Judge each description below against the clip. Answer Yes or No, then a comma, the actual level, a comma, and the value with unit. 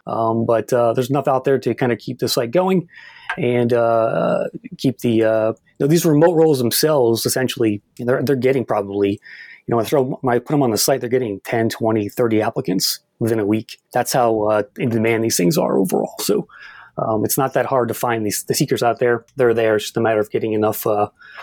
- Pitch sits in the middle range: No, low, 115 Hz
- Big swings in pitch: No, average, 2.9 semitones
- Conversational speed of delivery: No, fast, 230 wpm